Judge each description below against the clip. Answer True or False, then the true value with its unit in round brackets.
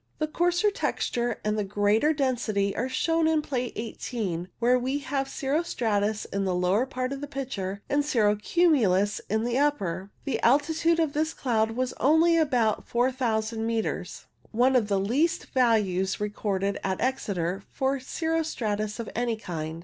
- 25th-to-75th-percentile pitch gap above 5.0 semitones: True (5.4 semitones)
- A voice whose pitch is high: True (240 Hz)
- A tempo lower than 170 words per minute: True (160 wpm)